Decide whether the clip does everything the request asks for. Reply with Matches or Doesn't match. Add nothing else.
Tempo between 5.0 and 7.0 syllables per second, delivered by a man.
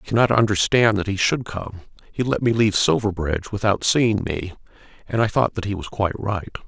Matches